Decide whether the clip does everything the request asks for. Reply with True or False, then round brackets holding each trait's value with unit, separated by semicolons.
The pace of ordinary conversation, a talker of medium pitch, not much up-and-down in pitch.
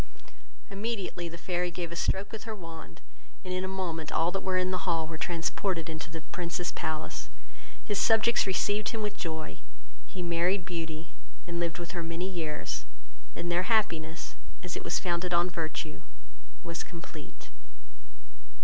True (165 wpm; 175 Hz; 2.3 semitones)